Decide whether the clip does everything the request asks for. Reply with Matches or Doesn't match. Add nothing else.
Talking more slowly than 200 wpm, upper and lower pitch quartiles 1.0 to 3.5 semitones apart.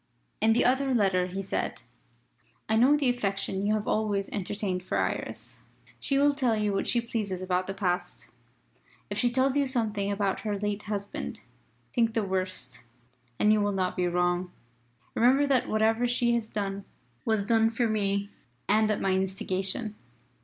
Matches